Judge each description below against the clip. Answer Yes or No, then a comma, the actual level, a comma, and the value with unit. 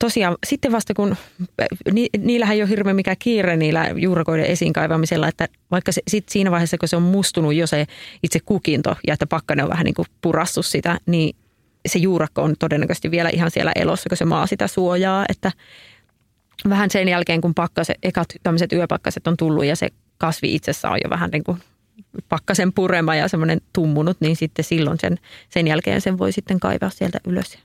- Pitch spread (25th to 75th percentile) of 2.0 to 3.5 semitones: Yes, average, 2.9 semitones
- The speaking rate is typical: No, fast, 190 wpm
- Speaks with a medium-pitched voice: Yes, medium, 170 Hz